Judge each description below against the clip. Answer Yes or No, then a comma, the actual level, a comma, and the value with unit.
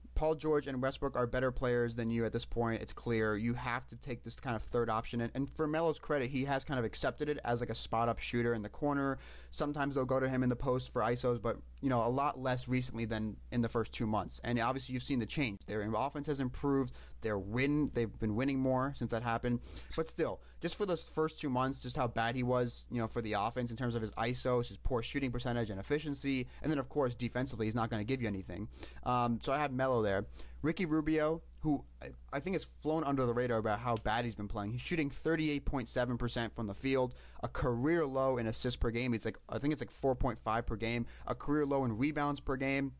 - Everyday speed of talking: No, fast, 240 wpm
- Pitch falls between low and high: No, low, 125 Hz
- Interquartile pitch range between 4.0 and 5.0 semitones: No, average, 3.0 semitones